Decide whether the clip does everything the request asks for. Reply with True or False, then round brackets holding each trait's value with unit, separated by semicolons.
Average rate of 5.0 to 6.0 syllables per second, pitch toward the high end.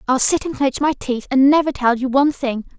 True (5.6 syllables/s; 270 Hz)